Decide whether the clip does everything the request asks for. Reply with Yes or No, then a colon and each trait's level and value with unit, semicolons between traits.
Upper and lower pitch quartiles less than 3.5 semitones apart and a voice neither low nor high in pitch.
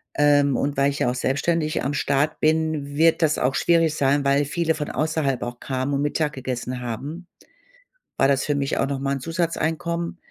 Yes: average, 2.7 semitones; medium, 145 Hz